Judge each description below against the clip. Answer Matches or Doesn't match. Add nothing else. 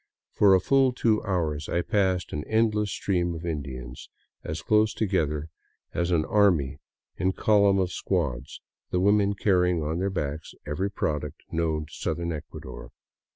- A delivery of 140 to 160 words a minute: Matches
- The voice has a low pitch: Matches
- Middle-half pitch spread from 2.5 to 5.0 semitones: Matches